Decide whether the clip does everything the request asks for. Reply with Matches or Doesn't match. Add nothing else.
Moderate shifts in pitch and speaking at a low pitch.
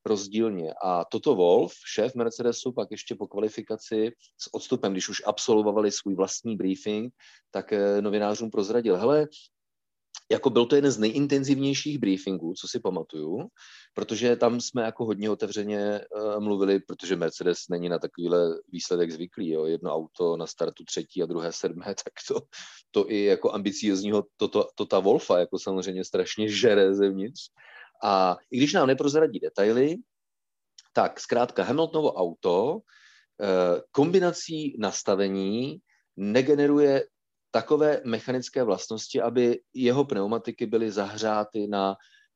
Matches